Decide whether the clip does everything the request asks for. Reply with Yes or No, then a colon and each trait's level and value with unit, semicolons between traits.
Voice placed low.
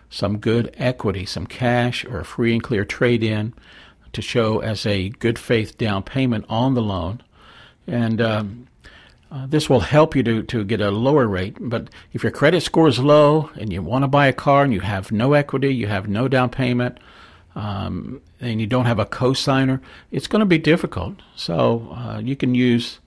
Yes: low, 120 Hz